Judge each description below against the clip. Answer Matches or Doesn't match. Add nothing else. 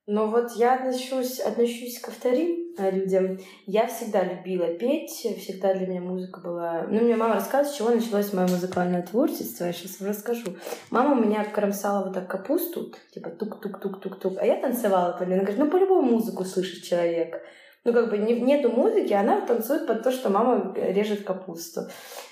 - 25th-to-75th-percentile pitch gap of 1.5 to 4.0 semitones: Doesn't match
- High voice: Matches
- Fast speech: Matches